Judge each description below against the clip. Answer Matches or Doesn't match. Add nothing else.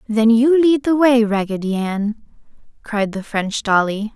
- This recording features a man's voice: Doesn't match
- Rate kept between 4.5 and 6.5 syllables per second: Doesn't match